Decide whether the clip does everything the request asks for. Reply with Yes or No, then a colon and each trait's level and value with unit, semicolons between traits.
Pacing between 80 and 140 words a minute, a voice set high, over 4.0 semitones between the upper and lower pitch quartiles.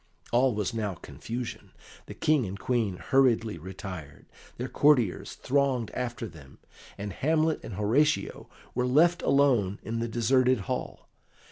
No: slow, 135 wpm; low, 115 Hz; average, 4.8 semitones